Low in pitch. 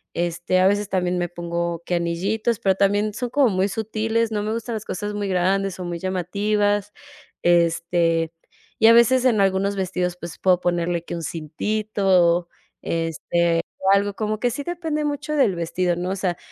No: high, 190 Hz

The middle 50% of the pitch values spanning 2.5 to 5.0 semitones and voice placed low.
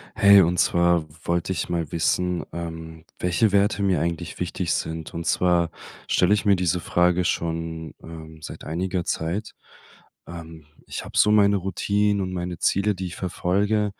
Yes: average, 2.9 semitones; very low, 90 Hz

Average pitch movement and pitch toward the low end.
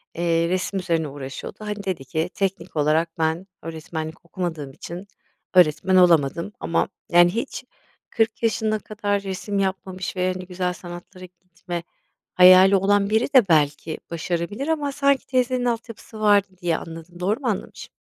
No: average, 3.6 semitones; medium, 185 Hz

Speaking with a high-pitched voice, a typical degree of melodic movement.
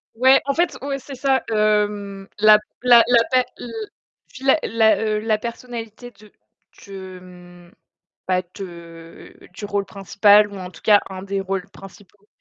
Yes: high, 210 Hz; average, 3.3 semitones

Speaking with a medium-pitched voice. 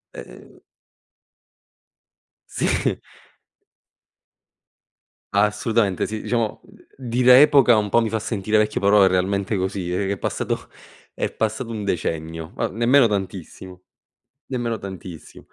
No: low, 105 Hz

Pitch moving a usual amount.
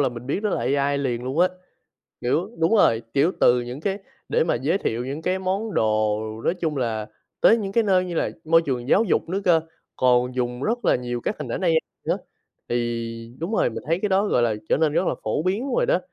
No: wide, 7.4 semitones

